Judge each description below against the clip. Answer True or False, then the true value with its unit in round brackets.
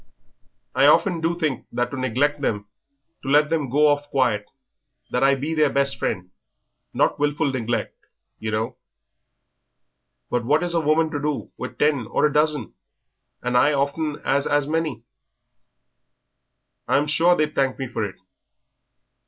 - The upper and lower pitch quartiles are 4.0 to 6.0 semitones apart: False (3.2 semitones)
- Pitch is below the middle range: False (145 Hz)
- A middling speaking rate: True (160 wpm)